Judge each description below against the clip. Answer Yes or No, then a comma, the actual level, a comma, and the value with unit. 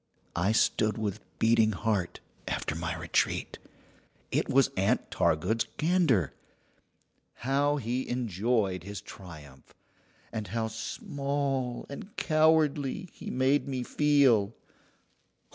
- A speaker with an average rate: No, slow, 105 wpm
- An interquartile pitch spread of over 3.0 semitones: Yes, wide, 5.5 semitones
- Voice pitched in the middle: No, low, 115 Hz